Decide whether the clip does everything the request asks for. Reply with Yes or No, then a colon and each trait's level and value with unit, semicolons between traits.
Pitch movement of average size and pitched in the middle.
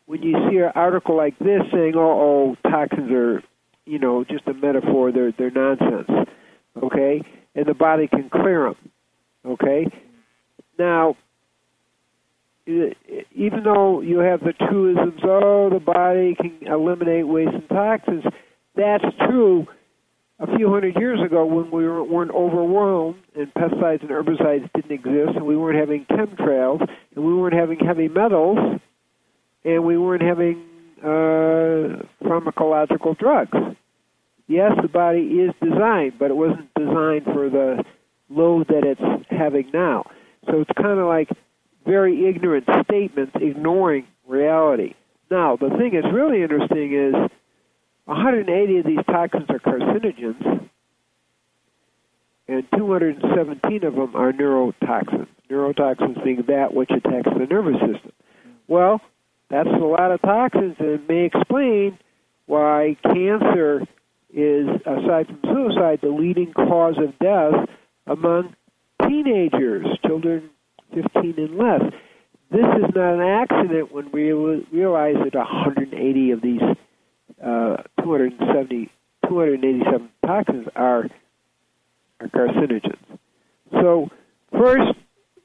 Yes: average, 4.5 semitones; medium, 160 Hz